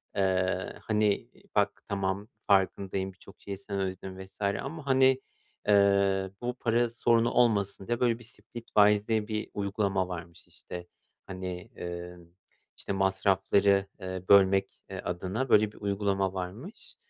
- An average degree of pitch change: No, narrow, 2.3 semitones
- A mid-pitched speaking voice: No, low, 100 Hz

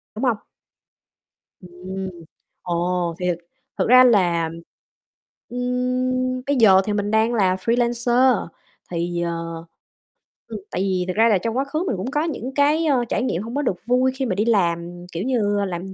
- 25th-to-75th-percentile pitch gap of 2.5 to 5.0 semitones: No, wide, 5.6 semitones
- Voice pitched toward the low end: No, high, 220 Hz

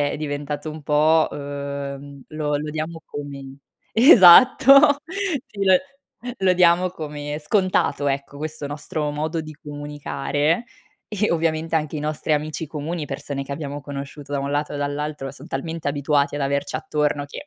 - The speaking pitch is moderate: Yes, medium, 150 Hz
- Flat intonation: Yes, narrow, 2.1 semitones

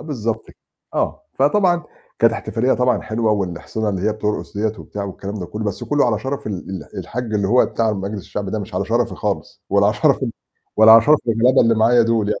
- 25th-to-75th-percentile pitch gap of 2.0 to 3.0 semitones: Yes, narrow, 2.6 semitones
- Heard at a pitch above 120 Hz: No, low, 110 Hz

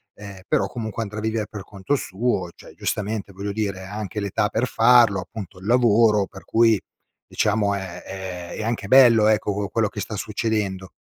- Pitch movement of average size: No, narrow, 2.2 semitones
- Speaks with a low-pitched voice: Yes, low, 105 Hz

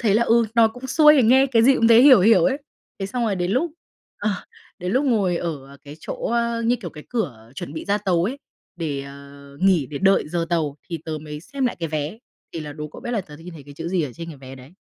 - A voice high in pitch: No, medium, 180 Hz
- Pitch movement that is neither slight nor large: No, wide, 7.5 semitones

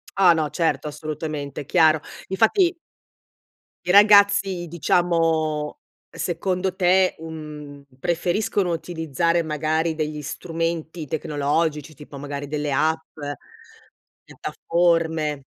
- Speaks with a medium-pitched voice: Yes, medium, 160 Hz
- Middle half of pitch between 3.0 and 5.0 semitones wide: No, narrow, 2.6 semitones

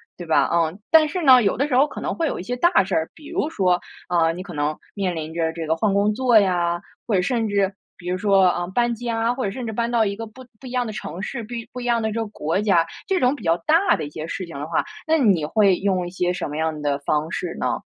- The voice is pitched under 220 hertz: Yes, high, 200 Hz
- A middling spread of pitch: No, wide, 5.9 semitones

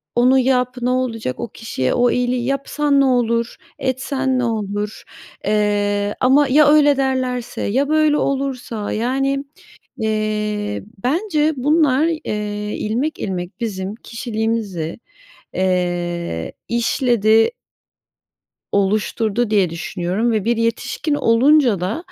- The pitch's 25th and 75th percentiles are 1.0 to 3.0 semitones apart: No, average, 4.3 semitones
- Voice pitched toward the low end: No, high, 235 Hz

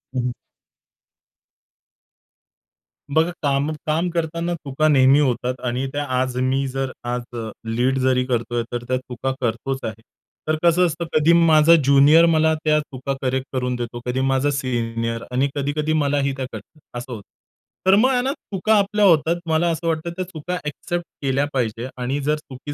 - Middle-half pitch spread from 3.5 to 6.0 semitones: Yes, average, 3.9 semitones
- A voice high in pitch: No, medium, 140 Hz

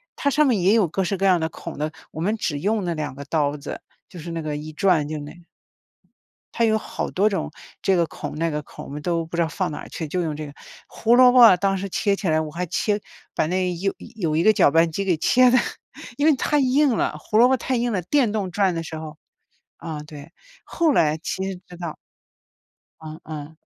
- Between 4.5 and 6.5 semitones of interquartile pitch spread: Yes, average, 5.2 semitones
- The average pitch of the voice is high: No, medium, 175 Hz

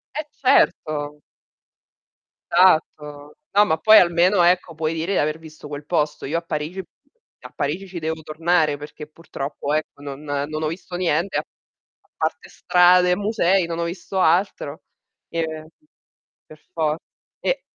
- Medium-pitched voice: Yes, medium, 160 Hz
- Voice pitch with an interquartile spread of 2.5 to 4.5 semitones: Yes, average, 2.9 semitones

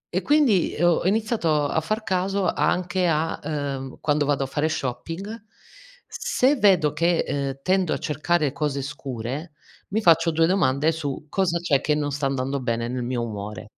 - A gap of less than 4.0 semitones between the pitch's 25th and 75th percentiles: No, average, 4.8 semitones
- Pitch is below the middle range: No, medium, 155 Hz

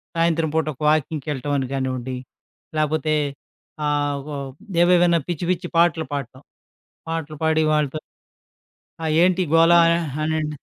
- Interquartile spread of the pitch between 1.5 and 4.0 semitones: Yes, narrow, 2.6 semitones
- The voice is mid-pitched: Yes, medium, 155 Hz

